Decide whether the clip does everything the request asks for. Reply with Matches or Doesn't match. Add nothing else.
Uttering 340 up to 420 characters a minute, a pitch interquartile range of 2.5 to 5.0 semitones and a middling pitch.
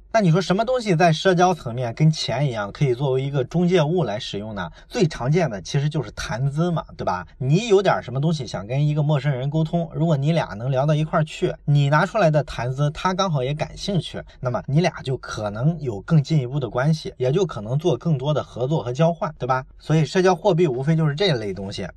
Matches